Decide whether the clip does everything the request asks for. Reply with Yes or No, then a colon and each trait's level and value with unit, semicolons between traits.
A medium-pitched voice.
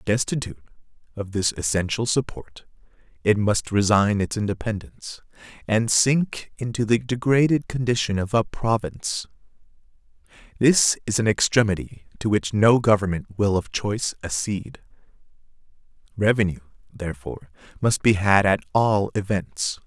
No: low, 105 Hz